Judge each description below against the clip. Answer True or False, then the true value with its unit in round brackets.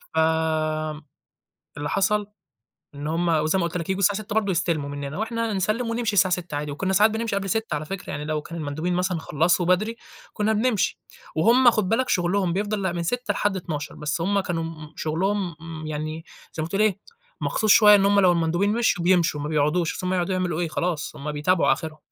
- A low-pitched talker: False (180 Hz)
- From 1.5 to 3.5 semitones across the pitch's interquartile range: False (4.4 semitones)